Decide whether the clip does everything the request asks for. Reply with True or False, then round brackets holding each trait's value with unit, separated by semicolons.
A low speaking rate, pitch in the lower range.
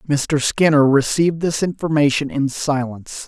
False (130 wpm; 145 Hz)